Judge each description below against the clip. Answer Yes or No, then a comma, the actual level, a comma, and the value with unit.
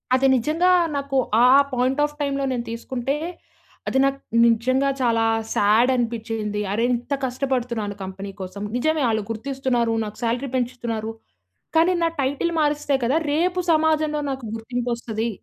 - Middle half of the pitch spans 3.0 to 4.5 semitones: Yes, average, 3.6 semitones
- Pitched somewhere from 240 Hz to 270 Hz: Yes, very high, 250 Hz